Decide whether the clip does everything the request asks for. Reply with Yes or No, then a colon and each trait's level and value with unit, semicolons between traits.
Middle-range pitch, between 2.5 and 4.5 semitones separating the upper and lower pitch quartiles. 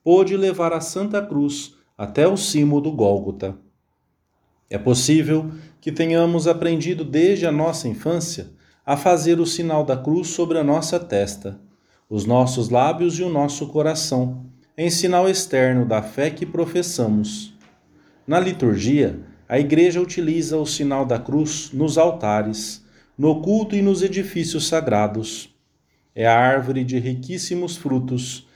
No: medium, 150 Hz; average, 5.3 semitones